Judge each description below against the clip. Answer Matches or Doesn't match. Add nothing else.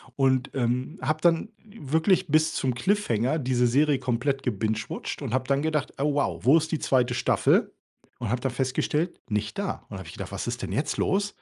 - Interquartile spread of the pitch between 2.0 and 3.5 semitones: Doesn't match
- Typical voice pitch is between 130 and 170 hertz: Matches